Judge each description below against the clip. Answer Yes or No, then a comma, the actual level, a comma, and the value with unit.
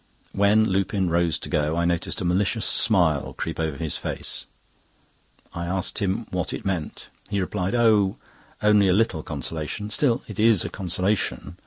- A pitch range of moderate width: Yes, average, 3.5 semitones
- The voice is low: Yes, very low, 95 Hz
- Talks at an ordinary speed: Yes, average, 160 wpm